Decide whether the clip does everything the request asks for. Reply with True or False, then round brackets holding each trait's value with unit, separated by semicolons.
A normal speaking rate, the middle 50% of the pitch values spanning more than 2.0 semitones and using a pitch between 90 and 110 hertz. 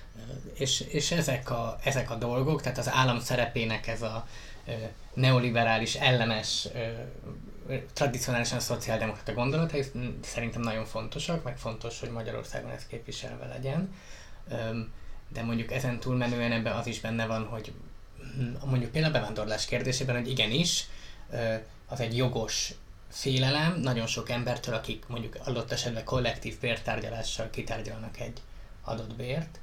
False (125 wpm; 2.5 semitones; 120 Hz)